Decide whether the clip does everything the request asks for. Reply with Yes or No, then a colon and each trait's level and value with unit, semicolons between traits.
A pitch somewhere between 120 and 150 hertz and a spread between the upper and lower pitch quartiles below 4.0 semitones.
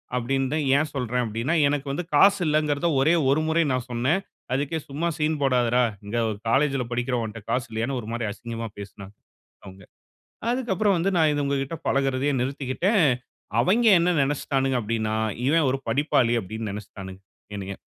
No: low, 135 Hz; average, 4.7 semitones